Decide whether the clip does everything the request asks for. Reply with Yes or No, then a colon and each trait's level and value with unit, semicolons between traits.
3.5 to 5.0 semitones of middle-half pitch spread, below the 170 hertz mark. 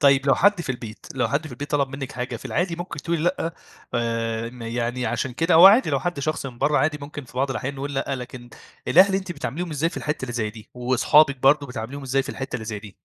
Yes: average, 4.1 semitones; low, 135 Hz